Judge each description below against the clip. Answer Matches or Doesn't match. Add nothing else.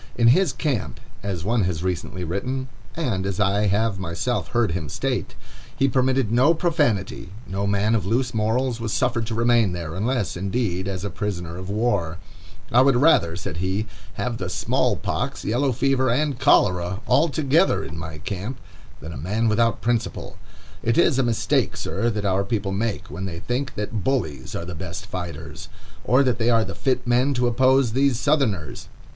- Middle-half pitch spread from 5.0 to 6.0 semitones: Matches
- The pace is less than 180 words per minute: Doesn't match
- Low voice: Matches